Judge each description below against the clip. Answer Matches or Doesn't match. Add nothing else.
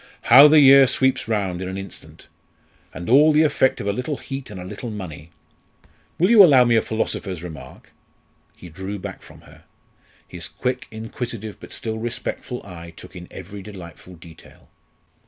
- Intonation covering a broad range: Matches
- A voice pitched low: Matches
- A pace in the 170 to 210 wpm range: Matches